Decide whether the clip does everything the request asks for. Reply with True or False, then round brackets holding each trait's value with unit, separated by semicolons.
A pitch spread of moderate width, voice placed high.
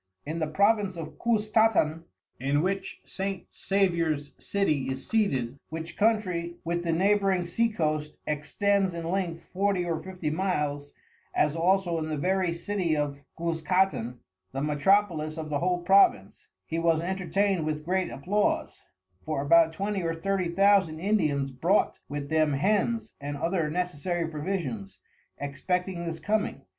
False (4.2 semitones; 170 Hz)